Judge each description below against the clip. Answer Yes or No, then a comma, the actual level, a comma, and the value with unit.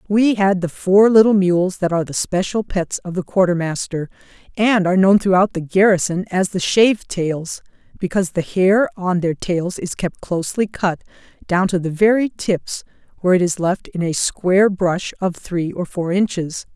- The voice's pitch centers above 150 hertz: Yes, medium, 185 Hz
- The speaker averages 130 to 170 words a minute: No, average, 185 wpm